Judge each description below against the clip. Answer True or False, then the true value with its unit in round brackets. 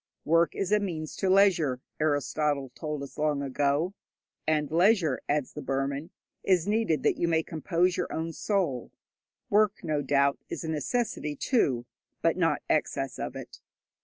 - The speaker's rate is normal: True (160 wpm)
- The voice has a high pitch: False (155 Hz)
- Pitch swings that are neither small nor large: True (4.2 semitones)